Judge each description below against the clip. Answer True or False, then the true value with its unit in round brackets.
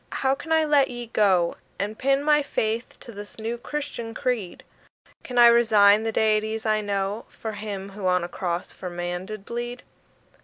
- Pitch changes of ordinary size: True (3.3 semitones)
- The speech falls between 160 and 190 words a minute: True (185 wpm)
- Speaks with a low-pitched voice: False (220 Hz)